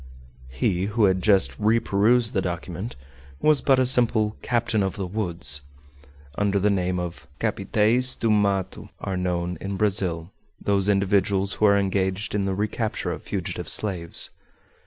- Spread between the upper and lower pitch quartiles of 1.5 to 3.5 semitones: Yes, narrow, 2.5 semitones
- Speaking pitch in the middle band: No, low, 100 Hz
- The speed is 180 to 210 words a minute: No, average, 150 wpm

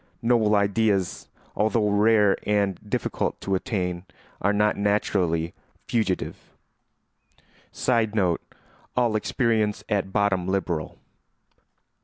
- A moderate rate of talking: No, slow, 90 wpm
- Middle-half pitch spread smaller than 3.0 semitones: Yes, narrow, 2.4 semitones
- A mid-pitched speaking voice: No, low, 100 Hz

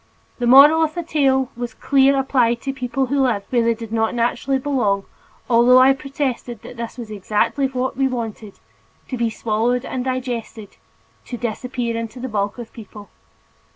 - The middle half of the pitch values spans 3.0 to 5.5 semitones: No, narrow, 2.6 semitones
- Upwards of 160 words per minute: Yes, average, 175 wpm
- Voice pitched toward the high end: Yes, high, 245 Hz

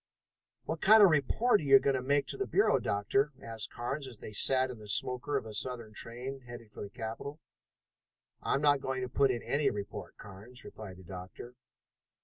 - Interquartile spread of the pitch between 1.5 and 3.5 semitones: No, average, 4.3 semitones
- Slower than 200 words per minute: No, fast, 205 wpm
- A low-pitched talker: Yes, low, 125 Hz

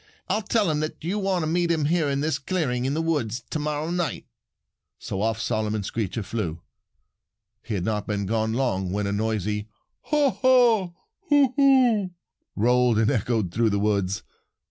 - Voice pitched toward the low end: Yes, low, 125 Hz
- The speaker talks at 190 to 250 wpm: No, average, 180 wpm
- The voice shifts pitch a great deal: Yes, wide, 8.5 semitones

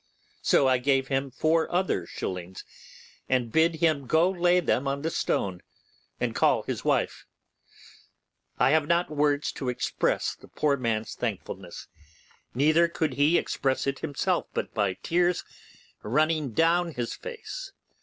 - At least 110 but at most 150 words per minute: Yes, average, 145 wpm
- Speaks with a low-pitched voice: No, medium, 145 Hz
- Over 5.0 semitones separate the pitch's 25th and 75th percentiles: No, average, 4.4 semitones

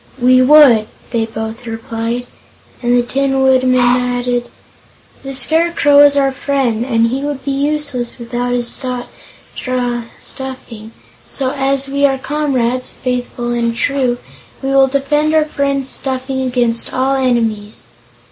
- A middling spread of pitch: No, narrow, 2.2 semitones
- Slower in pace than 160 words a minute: Yes, slow, 135 wpm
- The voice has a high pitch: Yes, very high, 255 Hz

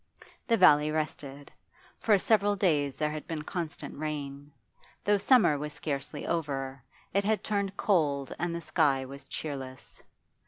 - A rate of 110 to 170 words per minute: Yes, average, 145 wpm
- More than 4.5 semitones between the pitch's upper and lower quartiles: Yes, average, 4.9 semitones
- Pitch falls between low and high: Yes, medium, 155 Hz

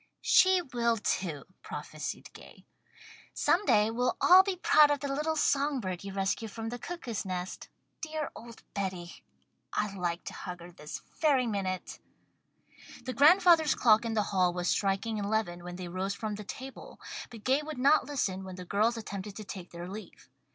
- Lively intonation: Yes, wide, 6.6 semitones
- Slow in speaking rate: No, average, 180 wpm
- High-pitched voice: Yes, high, 215 Hz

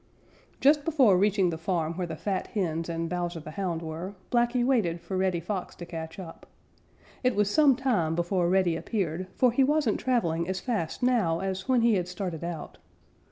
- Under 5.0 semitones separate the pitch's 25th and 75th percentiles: No, wide, 5.6 semitones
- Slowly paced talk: No, average, 195 wpm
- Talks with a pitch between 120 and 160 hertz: No, medium, 185 Hz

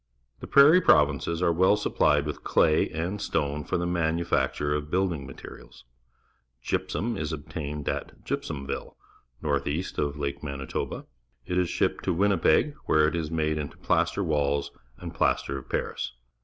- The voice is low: Yes, very low, 75 Hz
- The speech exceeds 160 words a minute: No, average, 155 wpm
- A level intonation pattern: No, average, 3.3 semitones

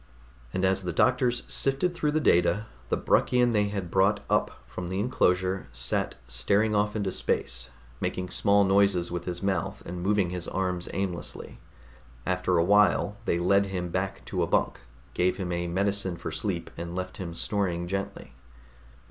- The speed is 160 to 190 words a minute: Yes, average, 170 wpm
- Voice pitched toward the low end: Yes, very low, 95 Hz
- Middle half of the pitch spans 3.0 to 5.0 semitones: No, narrow, 2.6 semitones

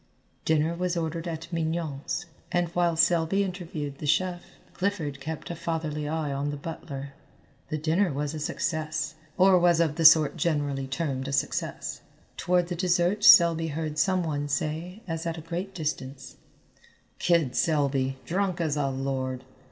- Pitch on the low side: No, medium, 160 Hz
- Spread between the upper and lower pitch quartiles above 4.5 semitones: No, average, 2.9 semitones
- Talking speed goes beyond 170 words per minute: No, average, 160 wpm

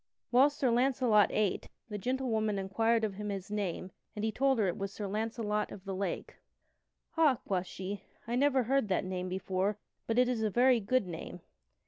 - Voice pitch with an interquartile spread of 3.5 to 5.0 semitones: Yes, average, 4.2 semitones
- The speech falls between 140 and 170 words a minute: No, average, 190 wpm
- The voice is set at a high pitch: Yes, high, 210 Hz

